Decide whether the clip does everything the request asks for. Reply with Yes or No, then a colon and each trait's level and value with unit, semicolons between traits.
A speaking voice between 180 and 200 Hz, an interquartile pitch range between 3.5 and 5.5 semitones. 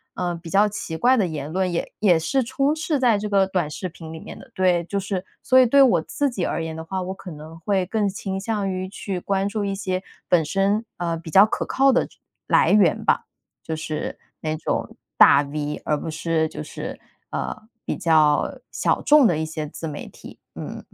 Yes: medium, 185 Hz; average, 4.2 semitones